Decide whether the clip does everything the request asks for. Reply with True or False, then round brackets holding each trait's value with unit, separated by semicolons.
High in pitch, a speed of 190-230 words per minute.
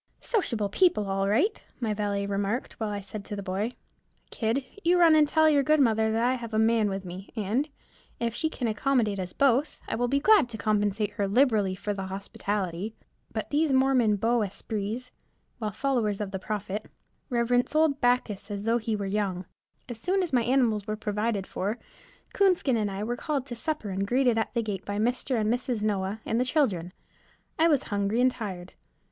True (220 Hz; 200 wpm)